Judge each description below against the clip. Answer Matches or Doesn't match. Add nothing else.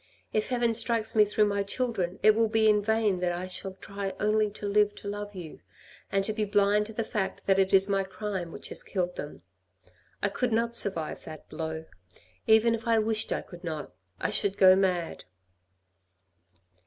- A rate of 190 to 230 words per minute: Matches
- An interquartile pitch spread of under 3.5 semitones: Matches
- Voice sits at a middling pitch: Doesn't match